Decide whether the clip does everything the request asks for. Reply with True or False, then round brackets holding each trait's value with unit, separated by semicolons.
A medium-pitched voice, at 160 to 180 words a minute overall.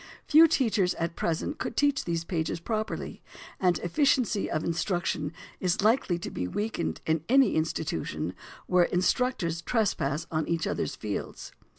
False (175 Hz; 145 wpm)